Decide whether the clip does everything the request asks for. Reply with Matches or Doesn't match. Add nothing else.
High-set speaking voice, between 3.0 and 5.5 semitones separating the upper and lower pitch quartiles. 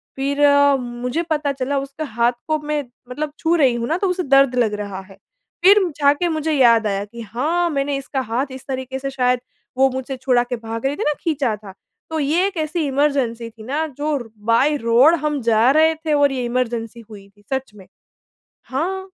Matches